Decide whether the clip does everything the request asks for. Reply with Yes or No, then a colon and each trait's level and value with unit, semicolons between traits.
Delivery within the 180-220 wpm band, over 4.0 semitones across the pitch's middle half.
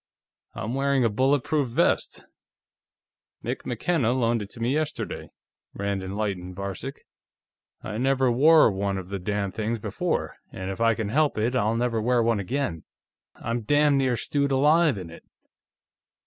No: average, 155 wpm; average, 5.2 semitones